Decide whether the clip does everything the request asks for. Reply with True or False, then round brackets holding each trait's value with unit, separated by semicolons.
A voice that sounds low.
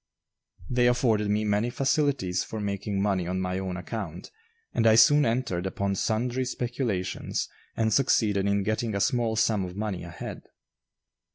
True (105 Hz)